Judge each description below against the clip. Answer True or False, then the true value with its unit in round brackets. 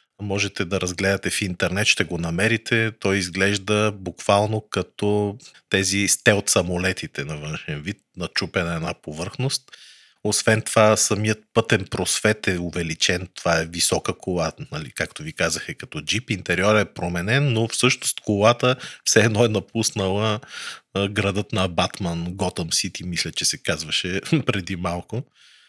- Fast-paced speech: False (145 wpm)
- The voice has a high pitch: False (100 Hz)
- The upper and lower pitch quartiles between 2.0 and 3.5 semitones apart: True (3.1 semitones)